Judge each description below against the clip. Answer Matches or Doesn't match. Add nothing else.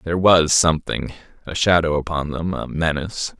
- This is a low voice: Matches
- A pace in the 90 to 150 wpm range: Matches